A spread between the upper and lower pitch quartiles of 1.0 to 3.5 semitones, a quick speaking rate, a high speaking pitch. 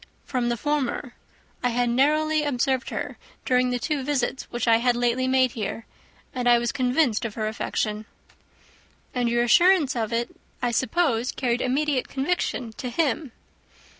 No: average, 2.7 semitones; average, 165 wpm; very high, 250 Hz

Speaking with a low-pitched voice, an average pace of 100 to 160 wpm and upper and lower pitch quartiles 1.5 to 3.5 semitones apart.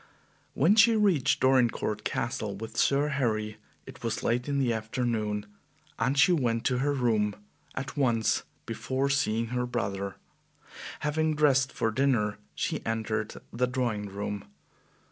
No: low, 120 Hz; average, 140 wpm; average, 4.2 semitones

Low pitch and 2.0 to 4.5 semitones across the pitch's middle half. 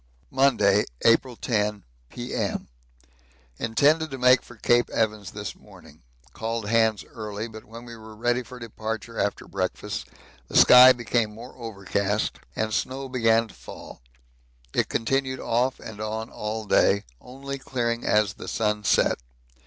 Yes: low, 115 Hz; average, 2.7 semitones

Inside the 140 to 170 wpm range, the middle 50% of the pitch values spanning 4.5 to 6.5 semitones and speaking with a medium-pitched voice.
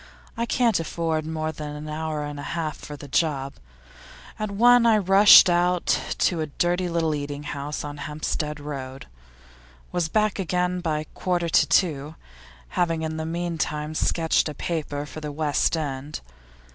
No: average, 165 wpm; average, 2.9 semitones; medium, 160 Hz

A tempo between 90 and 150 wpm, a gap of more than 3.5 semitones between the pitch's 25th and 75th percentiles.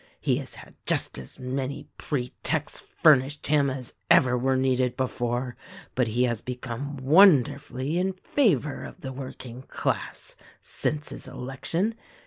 No: average, 140 wpm; average, 2.7 semitones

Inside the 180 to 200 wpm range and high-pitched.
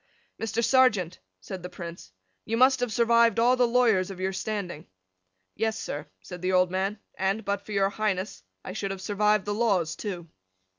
Yes: average, 185 wpm; high, 200 Hz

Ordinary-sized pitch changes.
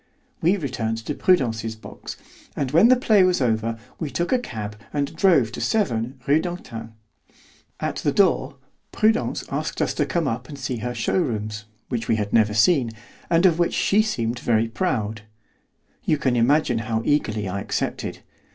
No: wide, 7.0 semitones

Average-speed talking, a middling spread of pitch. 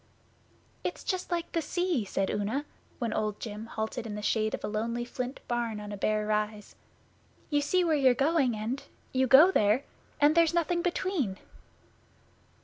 No: average, 170 wpm; wide, 6.6 semitones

